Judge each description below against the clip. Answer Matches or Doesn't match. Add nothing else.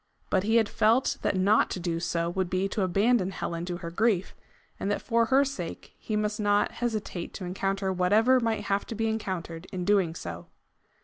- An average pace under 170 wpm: Doesn't match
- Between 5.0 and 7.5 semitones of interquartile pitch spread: Doesn't match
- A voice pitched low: Doesn't match